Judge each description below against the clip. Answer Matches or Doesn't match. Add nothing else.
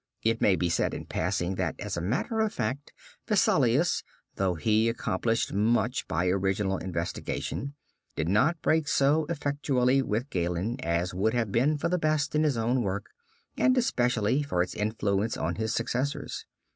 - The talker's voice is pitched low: Matches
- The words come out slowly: Doesn't match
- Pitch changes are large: Matches